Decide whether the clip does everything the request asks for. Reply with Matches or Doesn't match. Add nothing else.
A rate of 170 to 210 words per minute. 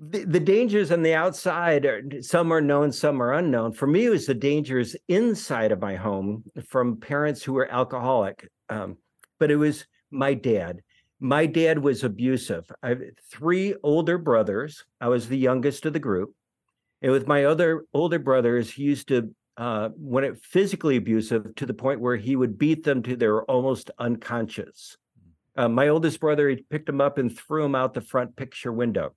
Matches